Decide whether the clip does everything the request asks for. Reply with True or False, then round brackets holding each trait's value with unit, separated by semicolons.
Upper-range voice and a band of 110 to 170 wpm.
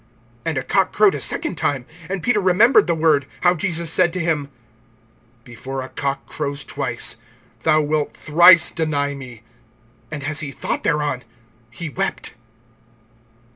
False (155 Hz; 150 wpm)